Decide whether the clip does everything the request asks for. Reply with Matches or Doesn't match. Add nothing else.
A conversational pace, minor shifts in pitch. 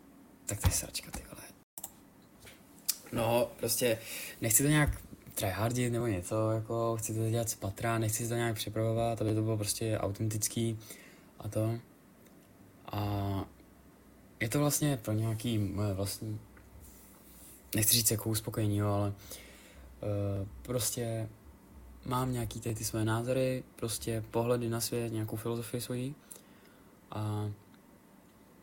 Matches